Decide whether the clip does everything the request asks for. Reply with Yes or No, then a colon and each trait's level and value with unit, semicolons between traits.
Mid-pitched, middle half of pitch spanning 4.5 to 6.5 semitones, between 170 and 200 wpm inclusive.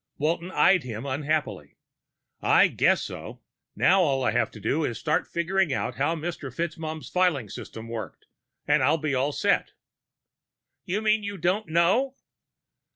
No: medium, 155 Hz; average, 5.1 semitones; average, 155 wpm